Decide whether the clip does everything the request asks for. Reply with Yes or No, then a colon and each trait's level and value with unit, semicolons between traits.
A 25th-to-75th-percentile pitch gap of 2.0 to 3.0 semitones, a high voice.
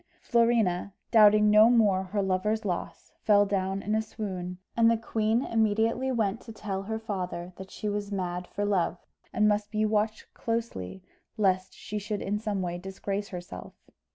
Yes: narrow, 2.4 semitones; high, 205 Hz